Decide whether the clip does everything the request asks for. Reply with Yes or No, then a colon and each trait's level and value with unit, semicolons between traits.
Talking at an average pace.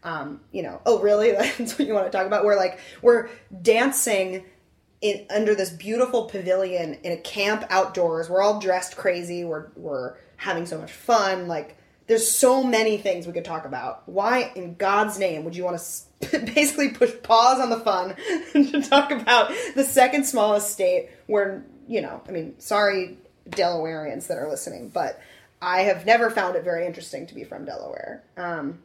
Yes: average, 185 wpm